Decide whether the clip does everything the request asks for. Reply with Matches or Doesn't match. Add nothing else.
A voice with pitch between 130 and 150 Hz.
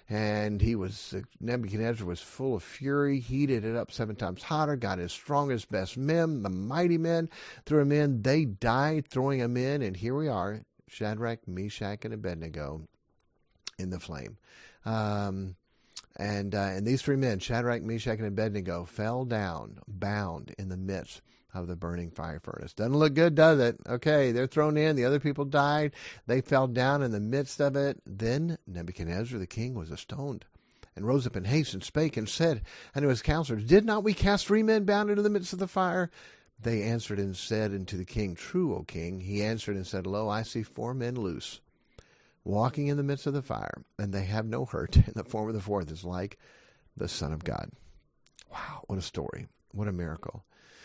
Doesn't match